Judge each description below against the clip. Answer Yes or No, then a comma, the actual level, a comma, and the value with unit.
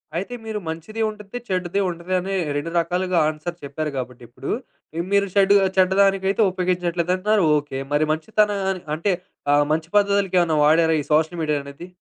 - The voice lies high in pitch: No, medium, 175 Hz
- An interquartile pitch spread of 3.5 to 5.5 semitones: Yes, average, 3.9 semitones